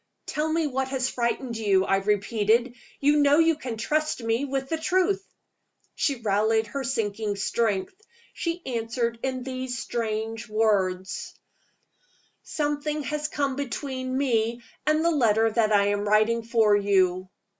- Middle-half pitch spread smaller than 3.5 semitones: No, average, 4.6 semitones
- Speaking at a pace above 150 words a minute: No, average, 145 wpm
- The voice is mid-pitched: No, high, 235 Hz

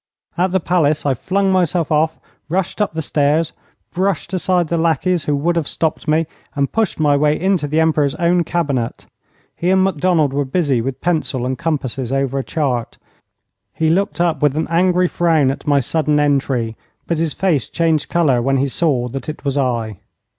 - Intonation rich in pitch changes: No, average, 3.9 semitones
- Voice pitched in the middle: Yes, medium, 155 Hz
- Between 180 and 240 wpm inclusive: Yes, average, 190 wpm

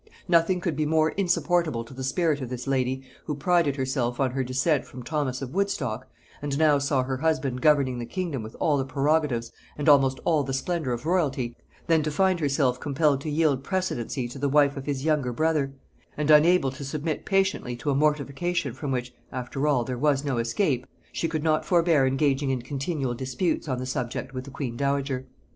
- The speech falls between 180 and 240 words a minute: Yes, average, 200 wpm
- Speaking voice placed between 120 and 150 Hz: Yes, medium, 140 Hz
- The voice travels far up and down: No, average, 3.2 semitones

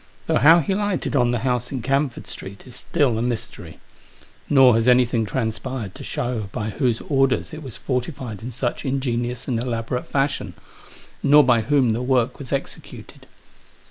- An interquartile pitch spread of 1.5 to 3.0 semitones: Yes, average, 2.7 semitones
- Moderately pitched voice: No, low, 125 Hz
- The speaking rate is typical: Yes, average, 170 wpm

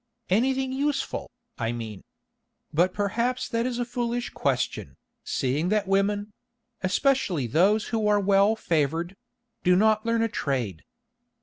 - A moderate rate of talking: No, slow, 120 wpm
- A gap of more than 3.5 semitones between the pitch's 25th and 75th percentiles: Yes, average, 5.3 semitones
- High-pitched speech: Yes, high, 205 Hz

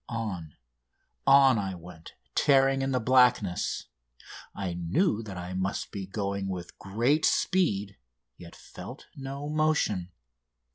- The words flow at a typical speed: No, slow, 125 wpm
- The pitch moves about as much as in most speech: No, wide, 6.5 semitones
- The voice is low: Yes, low, 105 Hz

